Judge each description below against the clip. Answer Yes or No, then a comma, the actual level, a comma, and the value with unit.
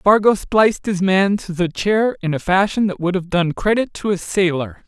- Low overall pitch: No, high, 190 Hz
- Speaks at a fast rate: Yes, fast, 220 wpm